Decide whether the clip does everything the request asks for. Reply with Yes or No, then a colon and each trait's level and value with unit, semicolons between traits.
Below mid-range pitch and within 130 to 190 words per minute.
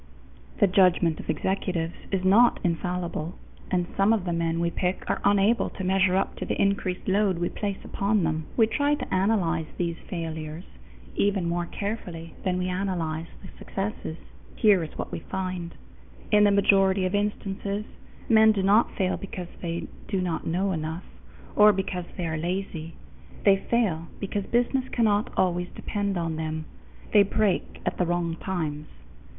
No: medium, 185 Hz; average, 165 wpm